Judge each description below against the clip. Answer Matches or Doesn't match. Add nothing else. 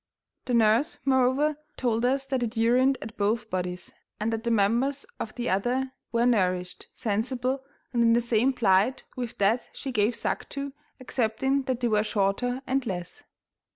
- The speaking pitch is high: Matches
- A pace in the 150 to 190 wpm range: Matches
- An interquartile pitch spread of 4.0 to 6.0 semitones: Doesn't match